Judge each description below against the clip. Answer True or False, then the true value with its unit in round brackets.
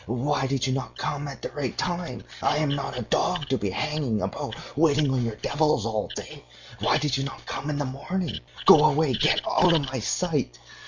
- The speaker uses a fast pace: True (215 wpm)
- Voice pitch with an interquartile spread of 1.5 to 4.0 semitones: True (2.9 semitones)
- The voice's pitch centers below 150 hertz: True (140 Hz)